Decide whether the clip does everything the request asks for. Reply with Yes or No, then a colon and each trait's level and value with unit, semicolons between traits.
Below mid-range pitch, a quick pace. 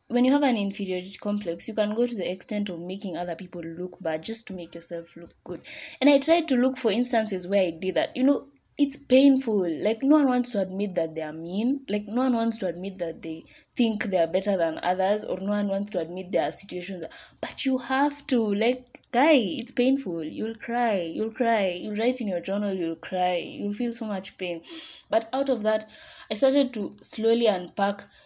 No: high, 210 Hz; fast, 225 wpm